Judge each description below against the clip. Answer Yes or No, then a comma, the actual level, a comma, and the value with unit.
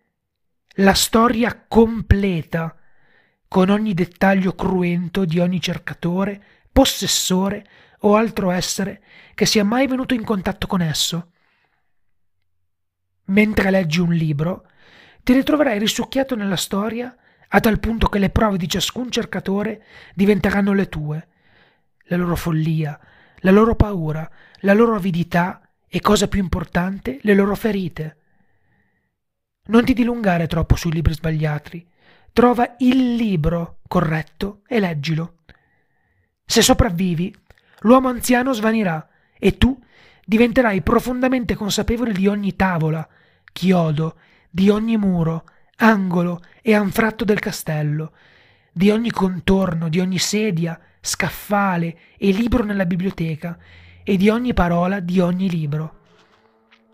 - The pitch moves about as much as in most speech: Yes, average, 4.6 semitones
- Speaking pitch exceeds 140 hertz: Yes, high, 190 Hz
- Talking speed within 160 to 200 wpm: No, average, 120 wpm